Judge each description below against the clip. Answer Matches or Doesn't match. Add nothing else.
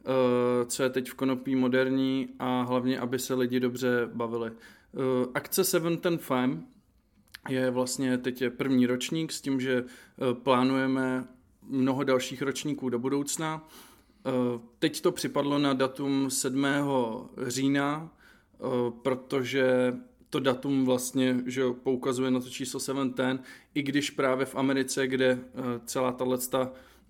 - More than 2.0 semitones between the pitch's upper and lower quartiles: Doesn't match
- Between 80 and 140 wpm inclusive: Matches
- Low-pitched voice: Matches